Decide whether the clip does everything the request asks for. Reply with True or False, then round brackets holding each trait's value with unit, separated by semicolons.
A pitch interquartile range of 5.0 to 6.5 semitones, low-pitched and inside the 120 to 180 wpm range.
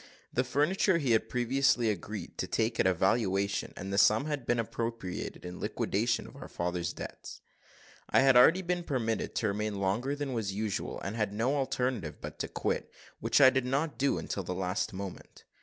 False (5.3 semitones; 115 Hz; 190 wpm)